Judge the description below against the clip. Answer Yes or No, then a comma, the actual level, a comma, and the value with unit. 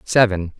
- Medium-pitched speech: No, low, 100 Hz